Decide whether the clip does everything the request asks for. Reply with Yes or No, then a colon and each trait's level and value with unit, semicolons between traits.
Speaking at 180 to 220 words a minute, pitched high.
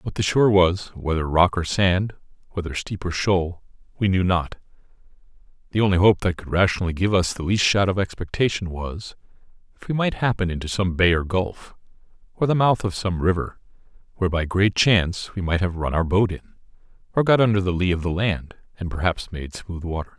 No: average, 200 wpm; very low, 95 Hz